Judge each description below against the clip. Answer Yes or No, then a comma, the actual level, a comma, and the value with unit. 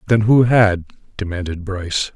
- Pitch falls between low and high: No, low, 100 Hz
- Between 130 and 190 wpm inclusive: Yes, average, 140 wpm